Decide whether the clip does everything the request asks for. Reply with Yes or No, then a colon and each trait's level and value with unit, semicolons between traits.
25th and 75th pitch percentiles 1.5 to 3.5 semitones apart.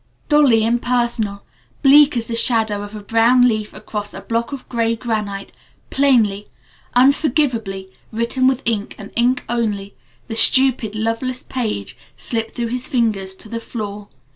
Yes: average, 3.0 semitones